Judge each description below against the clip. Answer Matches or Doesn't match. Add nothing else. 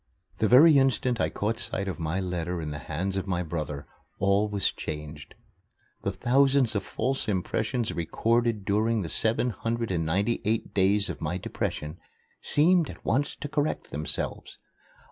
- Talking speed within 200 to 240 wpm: Doesn't match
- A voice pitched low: Matches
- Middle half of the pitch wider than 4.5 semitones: Matches